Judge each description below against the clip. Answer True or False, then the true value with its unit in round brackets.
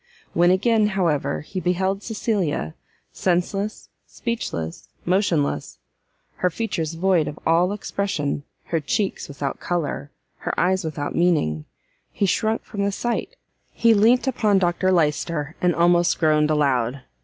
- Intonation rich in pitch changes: False (4.8 semitones)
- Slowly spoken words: True (130 wpm)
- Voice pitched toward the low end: False (175 Hz)